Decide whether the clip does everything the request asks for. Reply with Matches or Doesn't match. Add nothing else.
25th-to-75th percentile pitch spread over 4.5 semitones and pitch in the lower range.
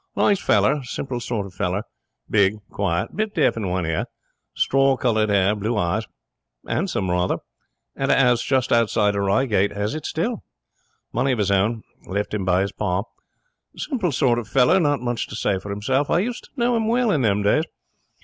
Matches